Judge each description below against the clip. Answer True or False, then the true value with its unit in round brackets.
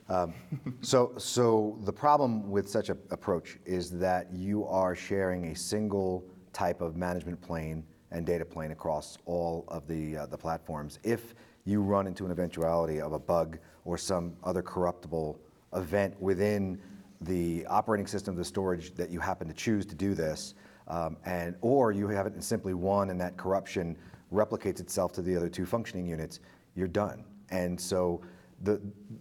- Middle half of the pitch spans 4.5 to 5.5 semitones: False (2.9 semitones)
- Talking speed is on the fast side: False (175 wpm)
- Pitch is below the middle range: True (90 Hz)